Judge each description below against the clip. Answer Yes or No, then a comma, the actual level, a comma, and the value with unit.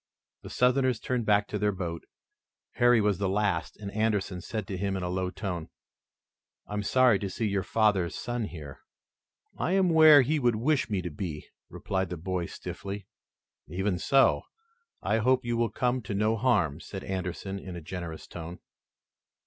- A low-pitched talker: Yes, low, 100 Hz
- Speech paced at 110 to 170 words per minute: No, average, 180 wpm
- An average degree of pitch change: Yes, average, 4.5 semitones